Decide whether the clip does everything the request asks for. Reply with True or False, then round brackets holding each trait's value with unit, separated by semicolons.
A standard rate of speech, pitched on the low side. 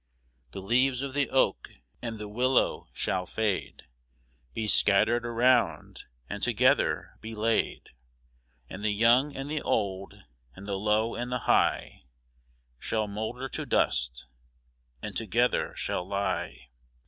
False (130 wpm; 110 Hz)